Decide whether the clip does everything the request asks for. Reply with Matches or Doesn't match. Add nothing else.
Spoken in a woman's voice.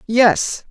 Matches